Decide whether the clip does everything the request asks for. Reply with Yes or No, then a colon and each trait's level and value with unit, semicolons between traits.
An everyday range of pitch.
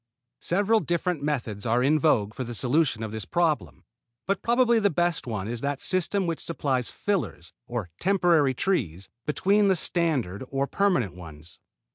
No: wide, 8.0 semitones